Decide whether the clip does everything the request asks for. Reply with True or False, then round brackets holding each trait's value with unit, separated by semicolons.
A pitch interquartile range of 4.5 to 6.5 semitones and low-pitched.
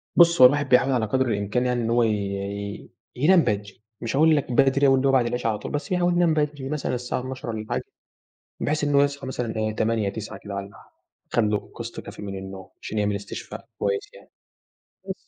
True (5.2 semitones; 120 Hz)